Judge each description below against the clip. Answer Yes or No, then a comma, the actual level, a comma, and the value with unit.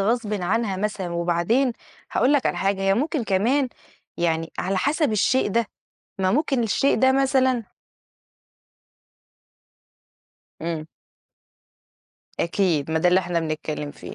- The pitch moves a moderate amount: No, wide, 6.9 semitones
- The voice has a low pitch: No, high, 200 Hz